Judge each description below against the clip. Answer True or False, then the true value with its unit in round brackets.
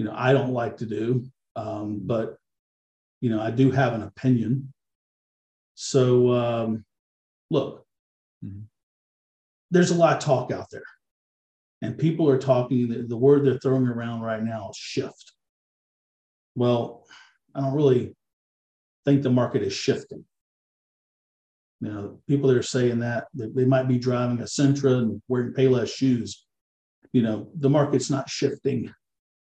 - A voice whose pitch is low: True (120 Hz)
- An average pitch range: True (4.0 semitones)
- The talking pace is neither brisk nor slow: True (150 wpm)